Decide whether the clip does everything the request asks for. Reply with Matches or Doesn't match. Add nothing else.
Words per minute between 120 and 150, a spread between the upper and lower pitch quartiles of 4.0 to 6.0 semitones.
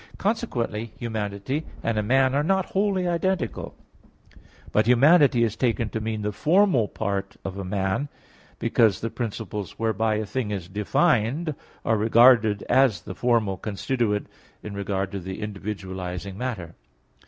Matches